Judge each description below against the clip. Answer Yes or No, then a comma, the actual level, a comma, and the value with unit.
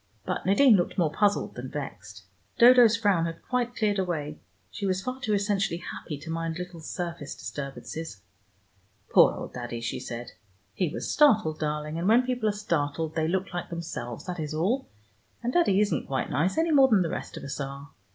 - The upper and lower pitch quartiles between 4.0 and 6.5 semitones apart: Yes, wide, 5.6 semitones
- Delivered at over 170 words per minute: Yes, average, 190 wpm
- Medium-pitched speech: Yes, medium, 175 Hz